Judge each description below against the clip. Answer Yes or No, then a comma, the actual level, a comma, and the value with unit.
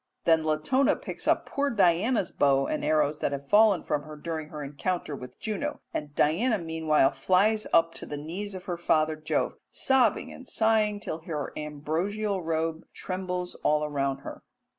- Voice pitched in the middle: Yes, medium, 165 Hz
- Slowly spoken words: No, average, 170 wpm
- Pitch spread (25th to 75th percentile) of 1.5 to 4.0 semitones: No, average, 5.2 semitones